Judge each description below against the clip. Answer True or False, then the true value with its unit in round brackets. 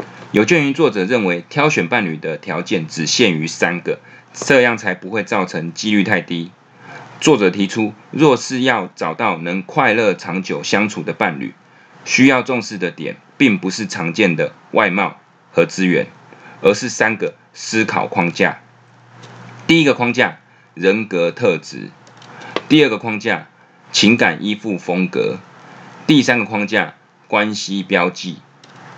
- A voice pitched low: True (95 Hz)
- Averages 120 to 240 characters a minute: True (215 characters per minute)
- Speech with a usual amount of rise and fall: True (3.8 semitones)